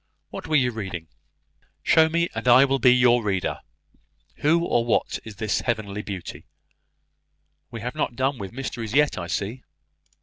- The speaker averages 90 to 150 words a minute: No, average, 165 wpm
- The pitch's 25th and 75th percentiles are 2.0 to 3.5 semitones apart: No, average, 4.6 semitones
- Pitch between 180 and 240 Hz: No, low, 120 Hz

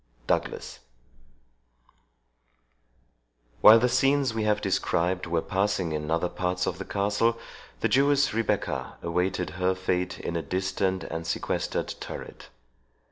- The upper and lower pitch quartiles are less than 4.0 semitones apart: Yes, average, 3.4 semitones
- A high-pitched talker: No, very low, 95 Hz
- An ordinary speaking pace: No, slow, 125 wpm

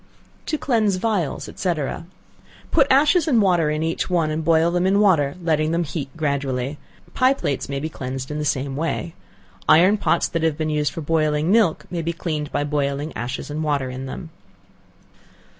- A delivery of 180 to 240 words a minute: Yes, average, 185 wpm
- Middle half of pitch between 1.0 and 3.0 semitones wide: No, average, 3.6 semitones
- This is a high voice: No, medium, 160 Hz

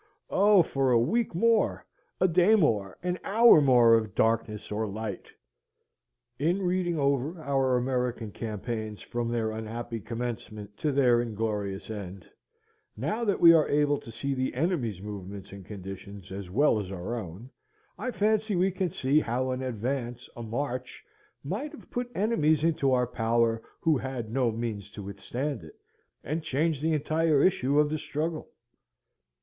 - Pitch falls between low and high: No, low, 125 Hz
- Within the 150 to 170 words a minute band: Yes, average, 160 wpm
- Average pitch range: No, wide, 6.2 semitones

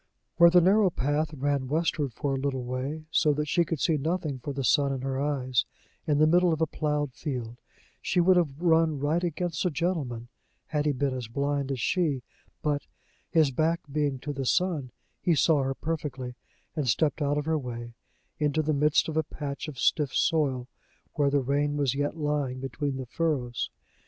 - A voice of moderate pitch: Yes, medium, 145 Hz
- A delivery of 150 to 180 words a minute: No, average, 195 wpm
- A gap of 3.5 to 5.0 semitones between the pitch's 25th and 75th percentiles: No, average, 2.9 semitones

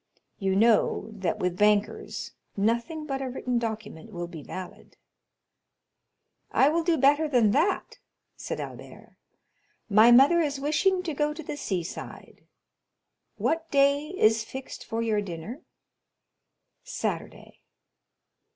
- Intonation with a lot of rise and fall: Yes, wide, 6.2 semitones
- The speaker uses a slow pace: Yes, slow, 125 wpm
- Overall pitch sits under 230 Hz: No, high, 245 Hz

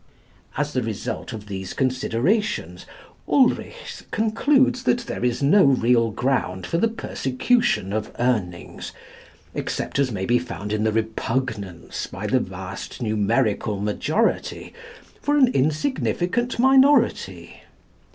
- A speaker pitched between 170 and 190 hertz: No, low, 130 Hz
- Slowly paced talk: Yes, slow, 120 wpm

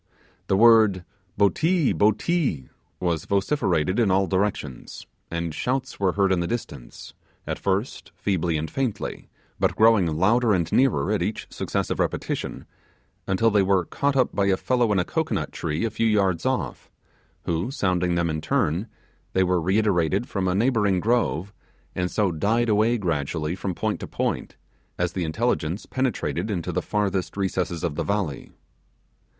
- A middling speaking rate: Yes, average, 160 wpm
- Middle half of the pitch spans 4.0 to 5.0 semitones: Yes, average, 4.3 semitones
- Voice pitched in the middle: No, very low, 95 Hz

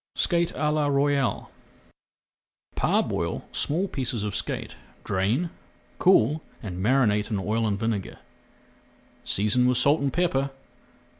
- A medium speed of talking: No, slow, 120 wpm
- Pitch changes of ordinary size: No, wide, 5.9 semitones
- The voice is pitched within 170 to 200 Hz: No, low, 125 Hz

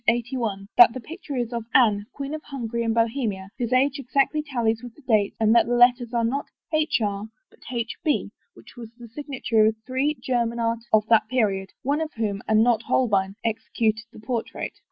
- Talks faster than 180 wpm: Yes, average, 195 wpm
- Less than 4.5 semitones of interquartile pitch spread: Yes, average, 2.8 semitones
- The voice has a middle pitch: No, high, 235 Hz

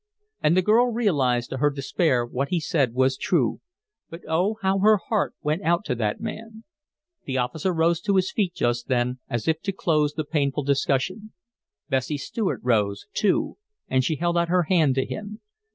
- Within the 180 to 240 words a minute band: Yes, average, 185 wpm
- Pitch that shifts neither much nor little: No, wide, 6.4 semitones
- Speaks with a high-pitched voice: No, medium, 160 Hz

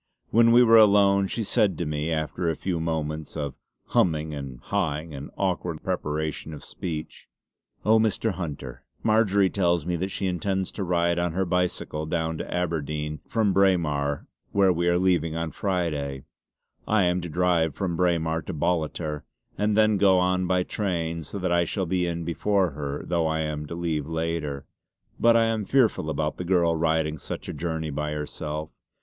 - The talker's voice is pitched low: Yes, very low, 85 Hz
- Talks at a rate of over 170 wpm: Yes, average, 180 wpm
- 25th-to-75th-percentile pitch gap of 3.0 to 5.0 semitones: Yes, average, 3.4 semitones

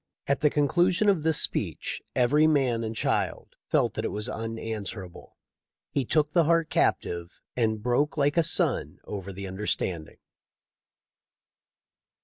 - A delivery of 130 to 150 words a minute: Yes, average, 140 wpm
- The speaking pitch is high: No, low, 125 Hz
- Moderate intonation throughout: No, wide, 6.3 semitones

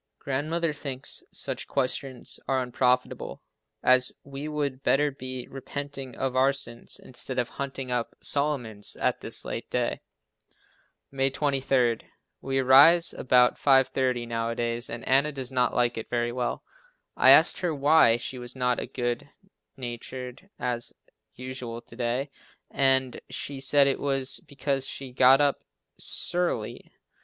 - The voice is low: Yes, low, 130 Hz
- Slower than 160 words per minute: Yes, average, 140 wpm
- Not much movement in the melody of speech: Yes, narrow, 2.0 semitones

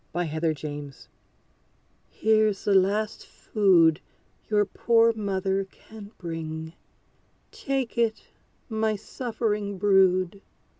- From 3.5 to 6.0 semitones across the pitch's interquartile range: Yes, average, 4.0 semitones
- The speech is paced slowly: Yes, slow, 95 wpm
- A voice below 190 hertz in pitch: No, high, 200 Hz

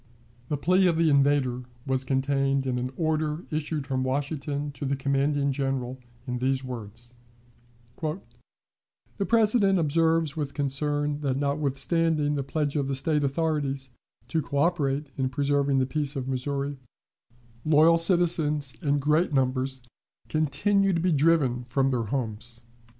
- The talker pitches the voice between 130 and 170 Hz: Yes, medium, 140 Hz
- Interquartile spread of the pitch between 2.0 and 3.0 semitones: Yes, average, 2.7 semitones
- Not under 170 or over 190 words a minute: No, average, 140 wpm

